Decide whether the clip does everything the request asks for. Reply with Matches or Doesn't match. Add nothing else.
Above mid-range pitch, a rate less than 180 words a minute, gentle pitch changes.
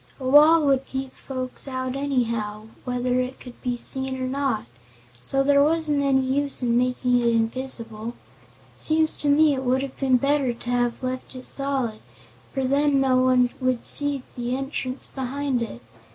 Matches